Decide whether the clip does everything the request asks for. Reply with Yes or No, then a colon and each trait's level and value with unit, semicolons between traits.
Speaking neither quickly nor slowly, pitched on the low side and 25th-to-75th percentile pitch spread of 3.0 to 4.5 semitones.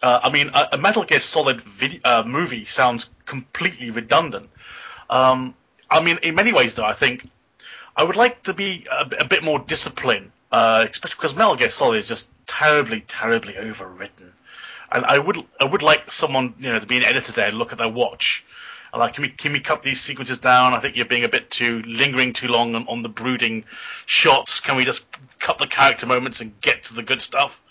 No: fast, 220 wpm; low, 125 Hz; average, 3.3 semitones